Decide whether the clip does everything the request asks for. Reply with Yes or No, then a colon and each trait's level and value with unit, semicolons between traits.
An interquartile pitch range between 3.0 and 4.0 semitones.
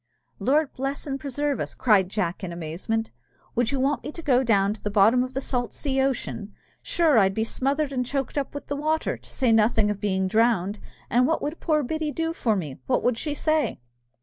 No: average, 5.3 semitones